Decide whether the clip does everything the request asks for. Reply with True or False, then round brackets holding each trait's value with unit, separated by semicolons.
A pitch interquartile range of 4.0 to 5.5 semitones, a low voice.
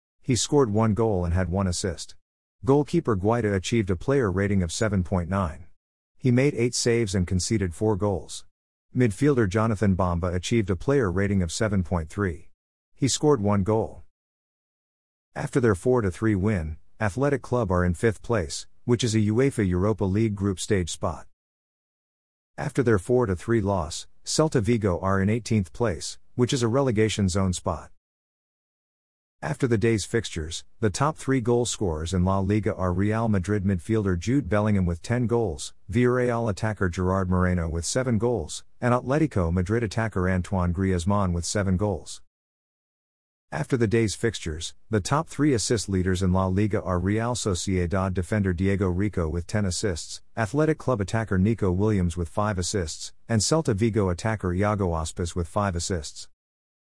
True (4.3 semitones; 100 Hz)